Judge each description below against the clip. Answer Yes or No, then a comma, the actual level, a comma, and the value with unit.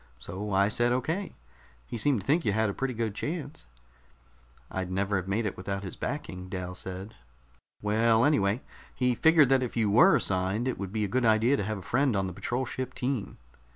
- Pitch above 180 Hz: No, low, 110 Hz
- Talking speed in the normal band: No, fast, 210 wpm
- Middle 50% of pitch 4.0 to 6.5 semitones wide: Yes, average, 4.8 semitones